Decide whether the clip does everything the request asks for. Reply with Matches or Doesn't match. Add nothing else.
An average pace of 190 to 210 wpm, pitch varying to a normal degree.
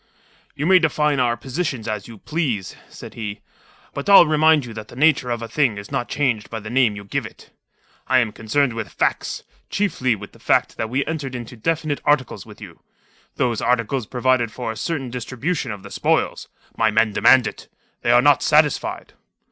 Matches